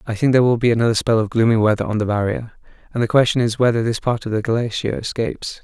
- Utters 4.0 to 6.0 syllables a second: No, 6.8 syllables/s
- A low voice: Yes, low, 115 Hz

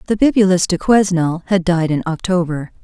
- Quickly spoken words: No, average, 170 wpm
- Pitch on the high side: No, medium, 180 Hz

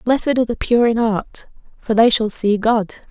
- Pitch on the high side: Yes, high, 225 Hz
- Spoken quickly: Yes, fast, 215 wpm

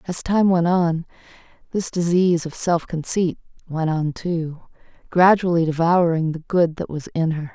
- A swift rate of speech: No, average, 160 wpm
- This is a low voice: No, medium, 170 Hz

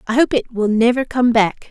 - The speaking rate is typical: No, fast, 245 wpm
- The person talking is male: No, female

